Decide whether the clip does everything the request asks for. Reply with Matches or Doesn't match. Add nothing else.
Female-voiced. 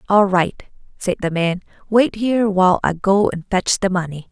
Matches